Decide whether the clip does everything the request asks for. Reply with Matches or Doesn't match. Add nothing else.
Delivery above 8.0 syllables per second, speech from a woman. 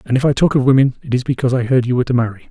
Doesn't match